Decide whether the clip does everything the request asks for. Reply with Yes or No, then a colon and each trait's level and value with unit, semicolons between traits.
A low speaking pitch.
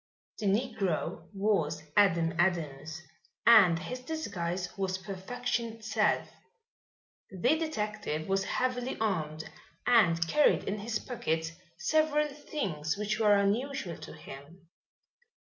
No: high, 200 Hz